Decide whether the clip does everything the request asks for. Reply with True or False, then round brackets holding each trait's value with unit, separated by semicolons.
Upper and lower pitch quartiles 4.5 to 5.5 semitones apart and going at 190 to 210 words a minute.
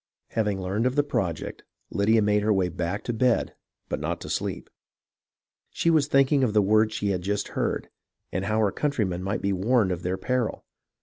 False (4.1 semitones; 195 wpm)